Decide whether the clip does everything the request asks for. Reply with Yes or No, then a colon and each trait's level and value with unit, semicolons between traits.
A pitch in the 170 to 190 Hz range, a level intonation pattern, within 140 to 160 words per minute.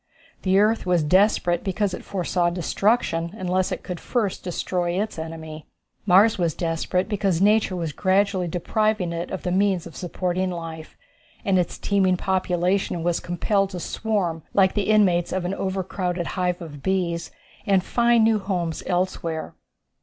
Yes: medium, 185 Hz; narrow, 2.3 semitones; average, 155 wpm